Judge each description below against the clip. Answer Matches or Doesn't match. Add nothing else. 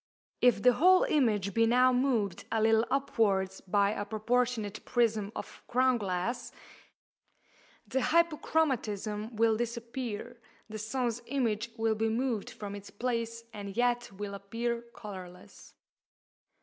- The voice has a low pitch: Doesn't match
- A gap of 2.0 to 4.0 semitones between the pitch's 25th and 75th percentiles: Matches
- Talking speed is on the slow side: Matches